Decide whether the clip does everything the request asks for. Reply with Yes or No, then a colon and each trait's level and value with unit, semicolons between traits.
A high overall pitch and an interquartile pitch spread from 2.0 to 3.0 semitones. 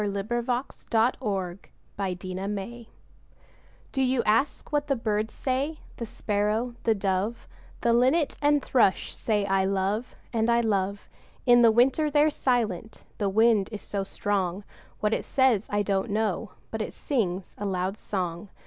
No: high, 215 Hz; average, 3.6 semitones